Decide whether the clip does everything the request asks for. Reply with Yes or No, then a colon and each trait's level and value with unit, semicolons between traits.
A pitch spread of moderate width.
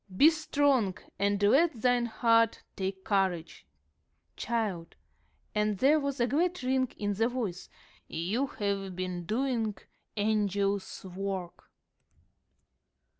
Yes: average, 4.7 semitones